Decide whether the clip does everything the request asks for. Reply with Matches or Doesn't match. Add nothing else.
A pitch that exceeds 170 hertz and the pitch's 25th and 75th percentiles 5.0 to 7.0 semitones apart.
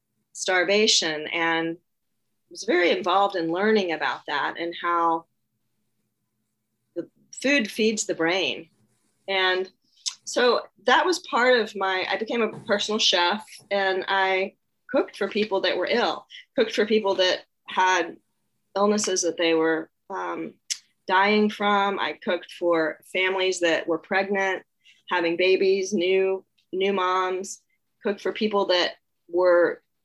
Doesn't match